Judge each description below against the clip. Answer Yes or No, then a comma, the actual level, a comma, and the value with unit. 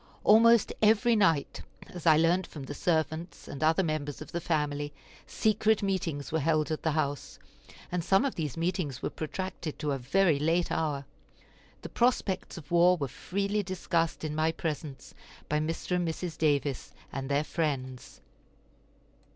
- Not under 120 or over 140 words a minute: No, average, 160 wpm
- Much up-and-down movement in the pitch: No, average, 3.7 semitones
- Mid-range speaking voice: Yes, medium, 160 Hz